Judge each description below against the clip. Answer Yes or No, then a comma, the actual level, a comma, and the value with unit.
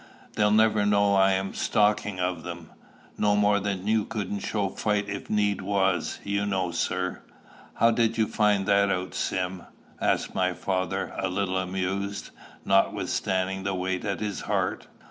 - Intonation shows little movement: Yes, narrow, 1.8 semitones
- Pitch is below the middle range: Yes, low, 100 Hz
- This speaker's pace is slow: No, average, 155 wpm